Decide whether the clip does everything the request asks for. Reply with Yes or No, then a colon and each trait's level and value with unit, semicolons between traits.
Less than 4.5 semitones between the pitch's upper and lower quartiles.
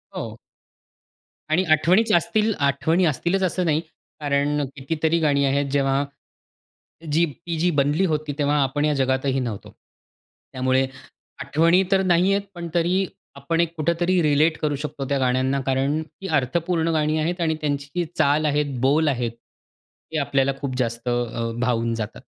Yes: average, 3.7 semitones